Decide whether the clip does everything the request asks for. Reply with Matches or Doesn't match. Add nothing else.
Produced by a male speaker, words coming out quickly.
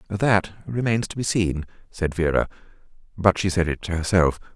Doesn't match